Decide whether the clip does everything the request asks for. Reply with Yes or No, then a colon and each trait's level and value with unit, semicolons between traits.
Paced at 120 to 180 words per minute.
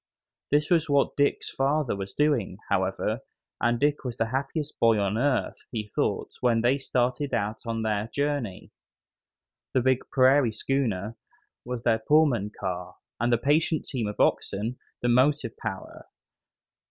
Yes: average, 150 wpm